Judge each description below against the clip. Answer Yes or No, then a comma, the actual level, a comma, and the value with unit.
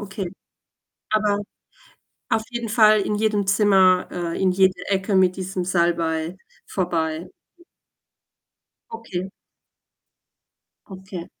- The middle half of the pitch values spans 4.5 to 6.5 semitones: No, narrow, 2.6 semitones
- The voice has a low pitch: No, high, 190 Hz